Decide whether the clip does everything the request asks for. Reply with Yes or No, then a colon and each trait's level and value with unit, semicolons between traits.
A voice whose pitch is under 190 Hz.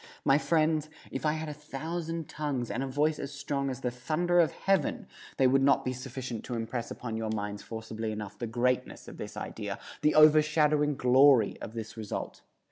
Yes: low, 135 Hz